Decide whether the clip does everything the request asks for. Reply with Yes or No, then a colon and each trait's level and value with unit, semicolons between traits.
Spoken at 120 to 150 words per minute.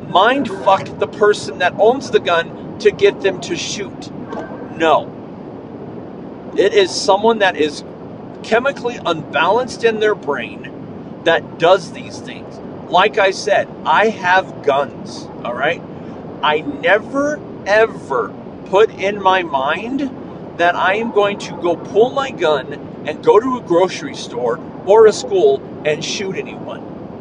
Yes: average, 140 wpm